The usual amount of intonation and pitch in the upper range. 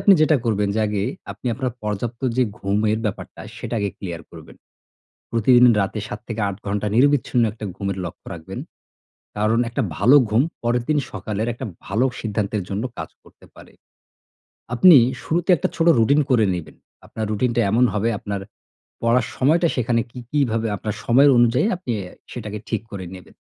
No: average, 3.4 semitones; low, 115 Hz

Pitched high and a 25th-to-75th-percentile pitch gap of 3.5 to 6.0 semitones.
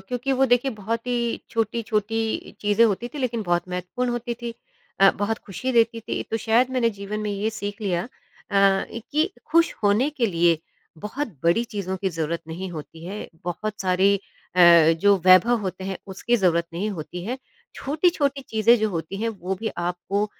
Yes: high, 210 Hz; average, 4.2 semitones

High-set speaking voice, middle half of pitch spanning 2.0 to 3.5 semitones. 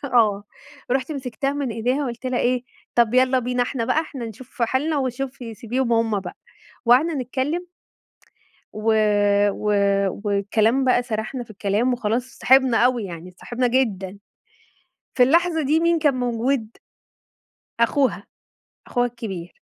Yes: high, 245 Hz; average, 2.9 semitones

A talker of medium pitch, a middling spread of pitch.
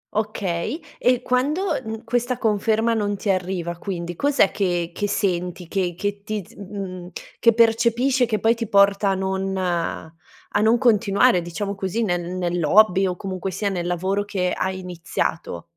No: high, 195 Hz; average, 3.7 semitones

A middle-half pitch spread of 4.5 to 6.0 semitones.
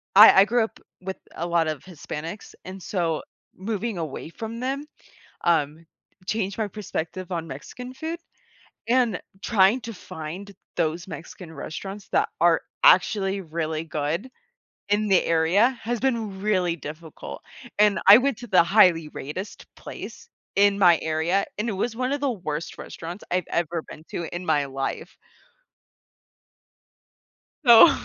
Yes: average, 5.1 semitones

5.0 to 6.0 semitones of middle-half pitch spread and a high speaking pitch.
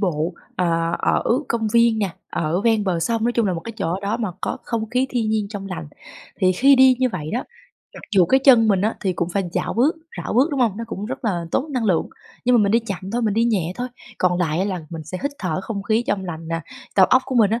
No: average, 4.4 semitones; high, 210 Hz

